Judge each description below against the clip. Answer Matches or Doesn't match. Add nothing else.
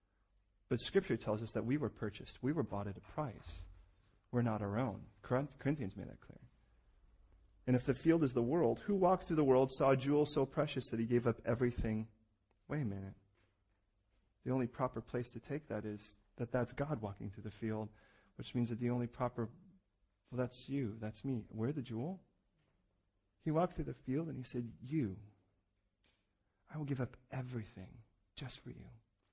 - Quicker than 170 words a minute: Matches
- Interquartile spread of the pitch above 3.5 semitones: Matches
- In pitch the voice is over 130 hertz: Doesn't match